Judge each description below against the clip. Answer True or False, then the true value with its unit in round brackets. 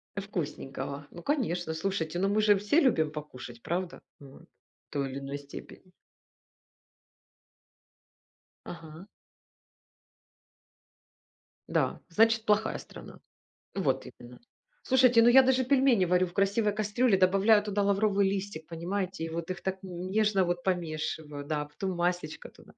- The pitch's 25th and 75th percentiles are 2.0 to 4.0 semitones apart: False (4.6 semitones)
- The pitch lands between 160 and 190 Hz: True (185 Hz)